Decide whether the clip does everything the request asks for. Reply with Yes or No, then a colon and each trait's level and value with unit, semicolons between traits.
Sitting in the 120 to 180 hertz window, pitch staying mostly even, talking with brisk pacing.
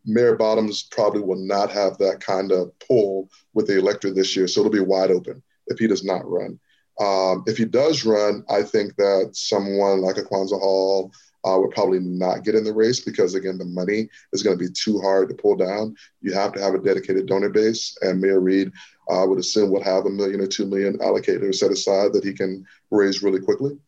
No: low, 100 Hz; narrow, 2.1 semitones; fast, 225 wpm